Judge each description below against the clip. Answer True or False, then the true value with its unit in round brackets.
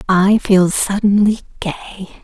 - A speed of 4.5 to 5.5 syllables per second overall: False (4.2 syllables/s)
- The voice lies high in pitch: True (195 Hz)